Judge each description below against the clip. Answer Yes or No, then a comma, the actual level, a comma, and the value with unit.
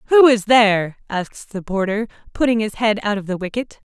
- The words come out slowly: No, average, 200 wpm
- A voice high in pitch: Yes, high, 215 Hz